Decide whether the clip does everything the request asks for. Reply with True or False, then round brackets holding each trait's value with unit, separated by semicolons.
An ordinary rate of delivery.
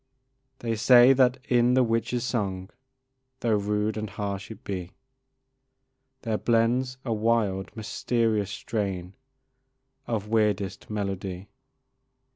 False (105 wpm)